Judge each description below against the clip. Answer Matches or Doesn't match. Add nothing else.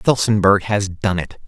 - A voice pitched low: Matches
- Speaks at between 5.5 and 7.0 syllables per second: Doesn't match